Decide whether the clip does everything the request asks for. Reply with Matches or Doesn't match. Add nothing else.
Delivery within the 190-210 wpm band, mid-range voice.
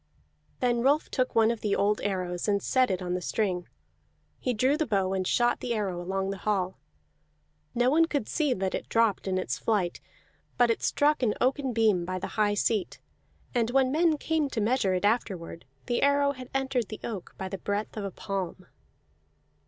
Doesn't match